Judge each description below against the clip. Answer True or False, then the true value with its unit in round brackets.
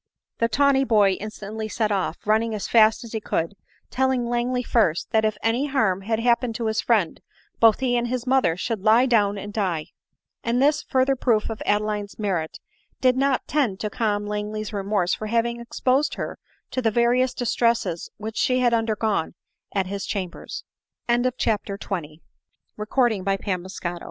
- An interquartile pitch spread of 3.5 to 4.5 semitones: False (2.9 semitones)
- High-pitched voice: True (225 Hz)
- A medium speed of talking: True (150 wpm)